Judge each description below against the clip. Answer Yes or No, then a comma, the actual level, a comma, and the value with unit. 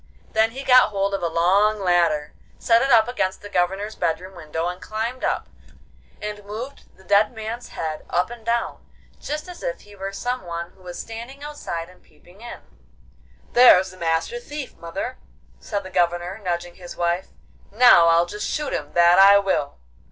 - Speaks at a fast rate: No, average, 180 wpm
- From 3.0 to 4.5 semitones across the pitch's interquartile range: No, average, 4.9 semitones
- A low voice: No, high, 195 Hz